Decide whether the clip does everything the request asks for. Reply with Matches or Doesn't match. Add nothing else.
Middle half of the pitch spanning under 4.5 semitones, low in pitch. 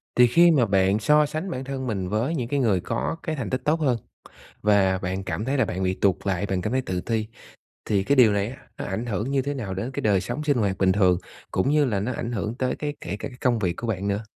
Doesn't match